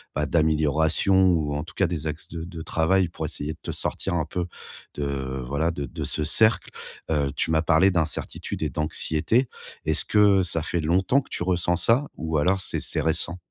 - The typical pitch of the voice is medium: No, very low, 80 Hz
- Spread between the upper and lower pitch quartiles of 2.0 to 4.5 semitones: Yes, average, 2.8 semitones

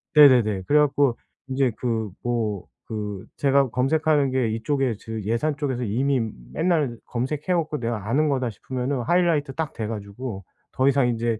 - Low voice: Yes, low, 130 Hz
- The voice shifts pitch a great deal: No, average, 4.1 semitones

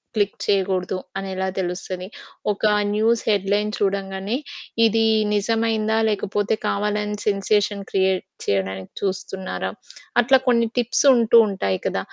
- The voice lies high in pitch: Yes, high, 200 Hz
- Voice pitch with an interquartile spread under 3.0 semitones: Yes, narrow, 2.5 semitones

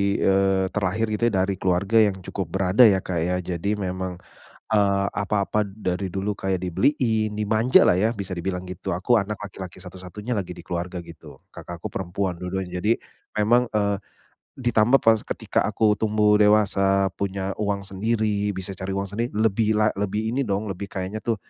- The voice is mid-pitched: No, low, 100 Hz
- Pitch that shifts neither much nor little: No, narrow, 2.3 semitones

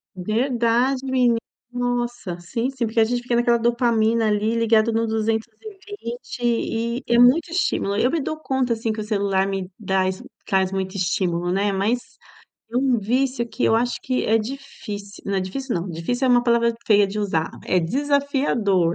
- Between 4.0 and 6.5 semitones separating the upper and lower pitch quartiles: No, average, 3.6 semitones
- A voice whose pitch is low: No, high, 230 Hz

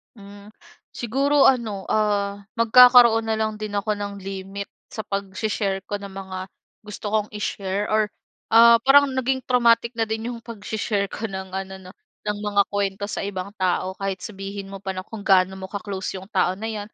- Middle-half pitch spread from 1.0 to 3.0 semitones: Yes, narrow, 2.4 semitones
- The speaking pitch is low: No, high, 205 Hz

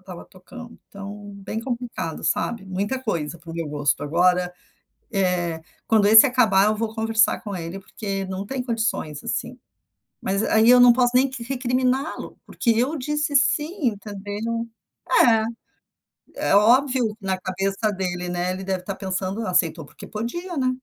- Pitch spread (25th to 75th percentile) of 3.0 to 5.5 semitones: Yes, average, 4.7 semitones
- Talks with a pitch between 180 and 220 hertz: Yes, high, 210 Hz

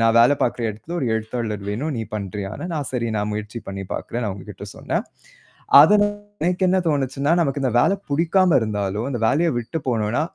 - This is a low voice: Yes, low, 120 Hz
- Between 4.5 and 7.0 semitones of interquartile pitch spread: Yes, wide, 5.6 semitones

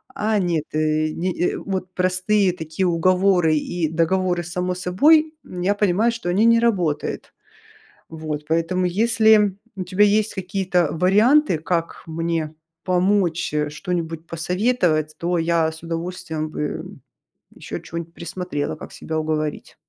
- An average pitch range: Yes, average, 3.0 semitones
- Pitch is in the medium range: Yes, medium, 180 Hz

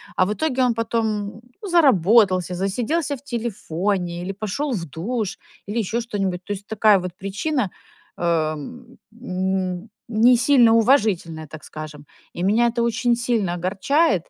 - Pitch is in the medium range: No, high, 210 Hz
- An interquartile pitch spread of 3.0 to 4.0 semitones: No, average, 4.6 semitones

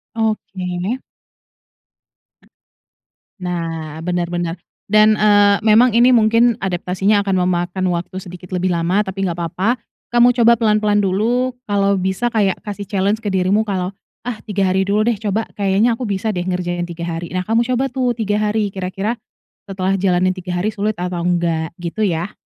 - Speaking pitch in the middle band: No, high, 195 Hz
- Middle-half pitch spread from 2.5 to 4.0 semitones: Yes, average, 3.2 semitones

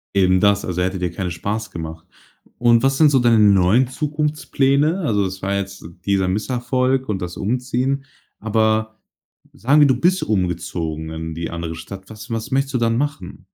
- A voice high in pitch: No, low, 110 Hz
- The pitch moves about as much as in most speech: No, wide, 6.1 semitones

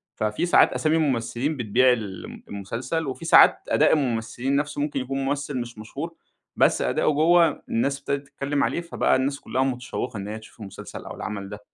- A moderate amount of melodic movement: Yes, average, 4.3 semitones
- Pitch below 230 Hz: Yes, low, 135 Hz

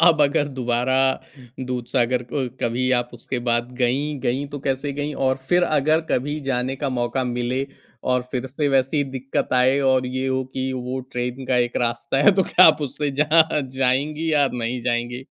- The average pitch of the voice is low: Yes, low, 130 Hz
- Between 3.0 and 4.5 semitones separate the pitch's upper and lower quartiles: No, narrow, 2.4 semitones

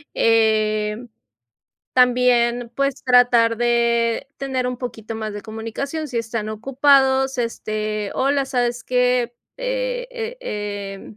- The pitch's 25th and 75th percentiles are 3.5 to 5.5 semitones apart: No, average, 2.9 semitones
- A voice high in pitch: Yes, high, 245 Hz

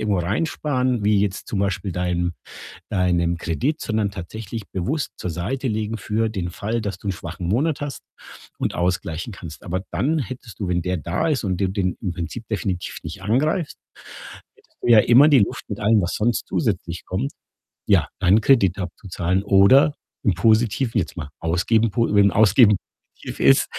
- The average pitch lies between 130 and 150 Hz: No, low, 100 Hz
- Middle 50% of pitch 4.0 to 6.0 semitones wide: Yes, average, 4.4 semitones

